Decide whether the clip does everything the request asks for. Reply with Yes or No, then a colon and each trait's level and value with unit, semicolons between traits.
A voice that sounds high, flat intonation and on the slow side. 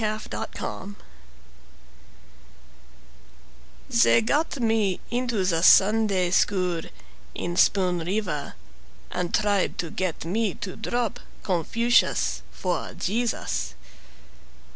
No: high, 195 Hz; average, 4.3 semitones; slow, 90 wpm